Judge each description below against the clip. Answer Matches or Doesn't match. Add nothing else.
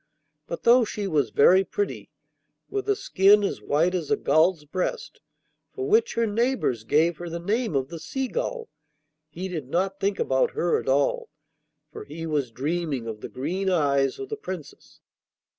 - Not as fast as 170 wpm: Doesn't match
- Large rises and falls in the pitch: Matches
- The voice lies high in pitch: Doesn't match